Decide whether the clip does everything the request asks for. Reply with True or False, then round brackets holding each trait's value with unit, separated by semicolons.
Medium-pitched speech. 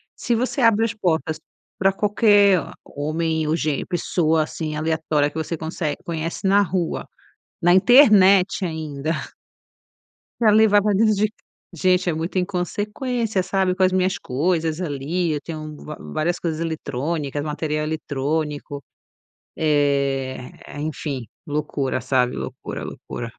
True (165 Hz)